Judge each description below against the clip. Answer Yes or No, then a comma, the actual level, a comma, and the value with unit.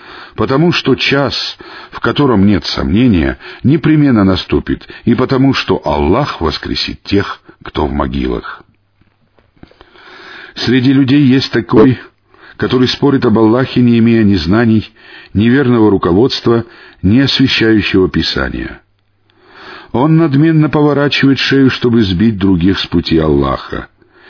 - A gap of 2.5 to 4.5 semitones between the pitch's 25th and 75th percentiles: No, average, 5.2 semitones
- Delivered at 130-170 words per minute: No, average, 115 wpm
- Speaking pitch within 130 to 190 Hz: No, low, 115 Hz